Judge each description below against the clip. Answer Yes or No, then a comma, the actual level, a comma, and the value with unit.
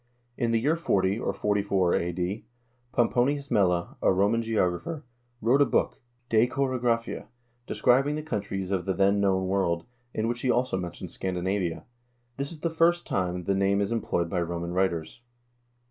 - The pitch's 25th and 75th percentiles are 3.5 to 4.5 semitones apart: No, average, 4.9 semitones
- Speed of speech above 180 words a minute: No, average, 165 wpm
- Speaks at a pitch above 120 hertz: No, low, 100 Hz